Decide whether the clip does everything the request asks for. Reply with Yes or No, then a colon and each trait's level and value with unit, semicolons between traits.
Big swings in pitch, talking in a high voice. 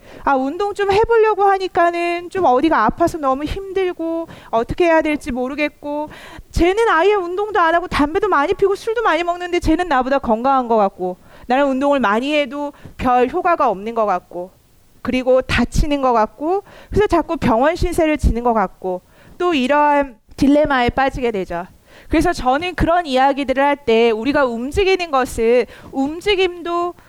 Yes: wide, 5.7 semitones; very high, 290 Hz